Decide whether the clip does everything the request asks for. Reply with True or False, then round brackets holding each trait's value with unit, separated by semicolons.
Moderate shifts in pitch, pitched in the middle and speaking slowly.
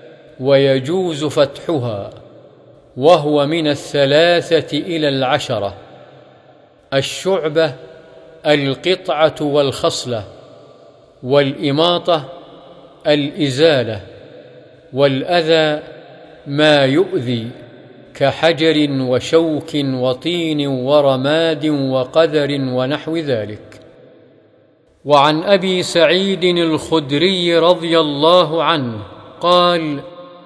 True (3.2 semitones; 150 Hz; 60 wpm)